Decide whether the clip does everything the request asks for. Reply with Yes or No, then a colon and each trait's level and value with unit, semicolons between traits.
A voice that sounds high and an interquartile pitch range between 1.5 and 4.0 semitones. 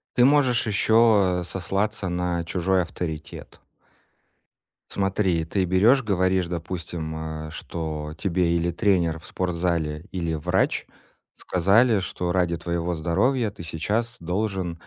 No: very low, 90 Hz; average, 3.1 semitones